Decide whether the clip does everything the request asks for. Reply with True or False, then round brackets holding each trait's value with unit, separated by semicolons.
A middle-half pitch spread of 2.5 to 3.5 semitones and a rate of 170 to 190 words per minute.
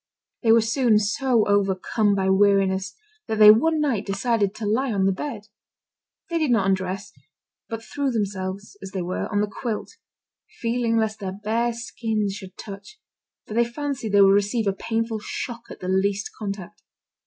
True (2.9 semitones; 175 wpm)